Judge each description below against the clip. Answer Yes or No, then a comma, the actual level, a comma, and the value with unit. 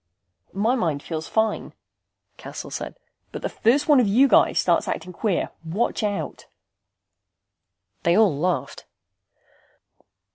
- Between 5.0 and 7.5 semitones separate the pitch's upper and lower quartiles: Yes, average, 5.3 semitones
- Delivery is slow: Yes, slow, 120 wpm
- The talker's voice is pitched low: No, high, 200 Hz